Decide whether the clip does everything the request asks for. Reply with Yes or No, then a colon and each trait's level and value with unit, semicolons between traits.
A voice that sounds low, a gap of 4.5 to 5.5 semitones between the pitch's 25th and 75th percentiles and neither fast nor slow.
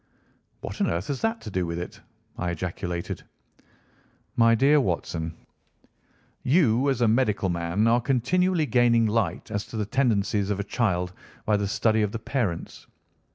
Yes: low, 110 Hz; average, 5.2 semitones; average, 160 wpm